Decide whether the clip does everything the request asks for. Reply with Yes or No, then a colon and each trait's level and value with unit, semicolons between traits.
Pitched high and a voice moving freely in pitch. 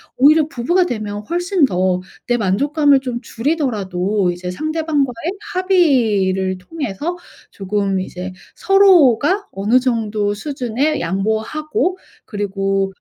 Yes: high, 235 Hz; wide, 7.8 semitones